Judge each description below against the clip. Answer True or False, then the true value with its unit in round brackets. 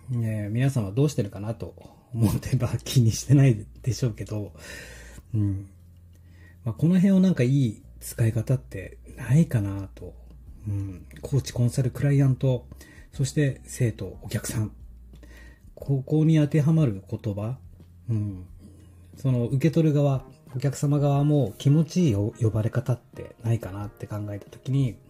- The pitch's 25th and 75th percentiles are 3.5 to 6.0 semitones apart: True (5.6 semitones)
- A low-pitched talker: True (115 Hz)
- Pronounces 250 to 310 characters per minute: True (295 characters per minute)